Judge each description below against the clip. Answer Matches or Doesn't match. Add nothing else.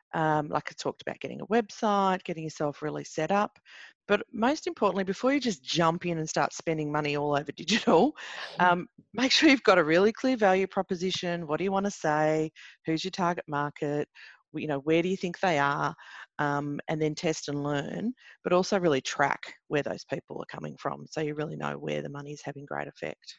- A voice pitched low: Doesn't match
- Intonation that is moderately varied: Matches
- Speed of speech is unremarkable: Doesn't match